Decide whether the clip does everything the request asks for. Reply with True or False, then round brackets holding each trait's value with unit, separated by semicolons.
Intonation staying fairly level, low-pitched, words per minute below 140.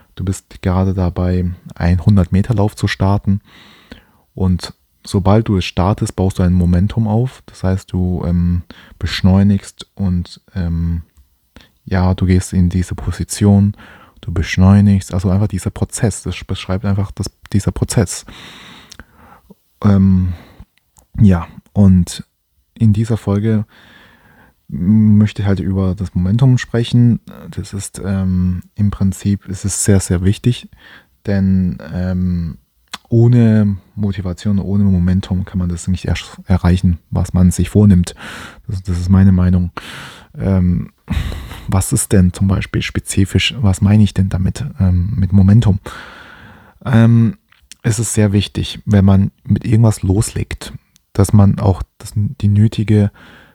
True (2.3 semitones; 95 Hz; 130 wpm)